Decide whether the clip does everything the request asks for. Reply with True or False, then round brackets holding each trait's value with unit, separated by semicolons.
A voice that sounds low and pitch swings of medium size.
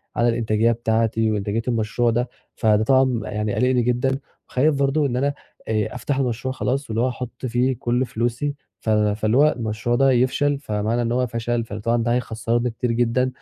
False (120 Hz; 2.3 semitones)